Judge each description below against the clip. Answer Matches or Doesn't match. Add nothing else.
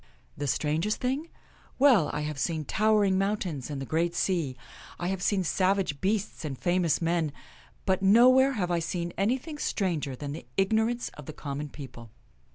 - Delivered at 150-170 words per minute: Doesn't match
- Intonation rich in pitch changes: Matches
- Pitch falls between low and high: Matches